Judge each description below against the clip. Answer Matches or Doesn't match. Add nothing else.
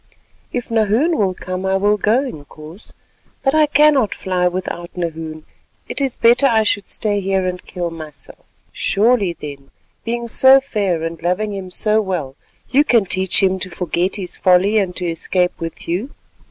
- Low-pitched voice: Doesn't match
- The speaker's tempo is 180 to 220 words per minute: Doesn't match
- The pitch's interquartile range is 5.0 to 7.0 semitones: Doesn't match